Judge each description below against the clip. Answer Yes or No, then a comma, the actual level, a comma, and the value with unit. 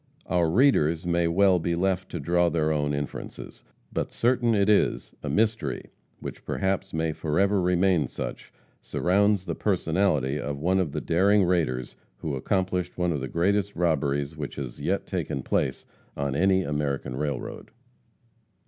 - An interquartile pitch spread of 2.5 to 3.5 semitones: No, average, 4.5 semitones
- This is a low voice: Yes, very low, 85 Hz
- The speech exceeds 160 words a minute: No, average, 155 wpm